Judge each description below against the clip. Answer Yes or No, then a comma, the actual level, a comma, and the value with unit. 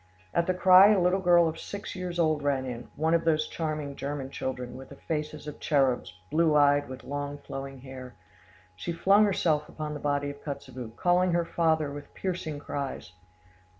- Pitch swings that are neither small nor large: Yes, average, 3.5 semitones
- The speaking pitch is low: No, medium, 150 Hz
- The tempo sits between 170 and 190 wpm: Yes, average, 185 wpm